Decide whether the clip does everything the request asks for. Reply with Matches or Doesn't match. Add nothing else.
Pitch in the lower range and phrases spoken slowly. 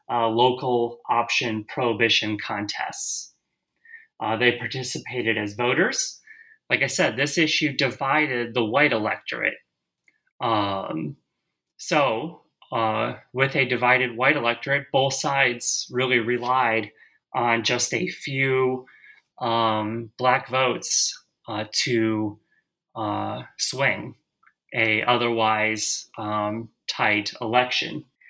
Matches